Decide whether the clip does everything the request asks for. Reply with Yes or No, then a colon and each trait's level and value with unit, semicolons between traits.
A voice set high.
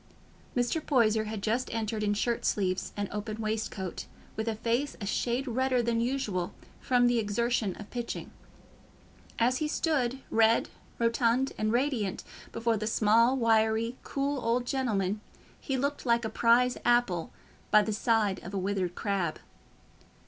Yes: high, 230 Hz